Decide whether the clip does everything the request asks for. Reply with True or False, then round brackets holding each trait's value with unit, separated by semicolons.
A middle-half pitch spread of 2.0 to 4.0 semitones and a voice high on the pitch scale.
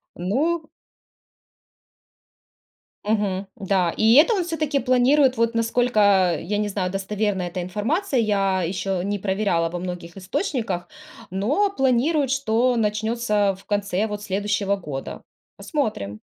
False (4.6 semitones; 210 Hz)